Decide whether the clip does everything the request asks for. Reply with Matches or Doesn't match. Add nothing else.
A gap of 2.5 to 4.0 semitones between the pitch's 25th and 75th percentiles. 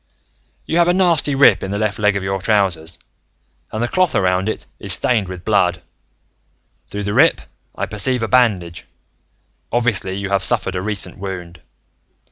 Doesn't match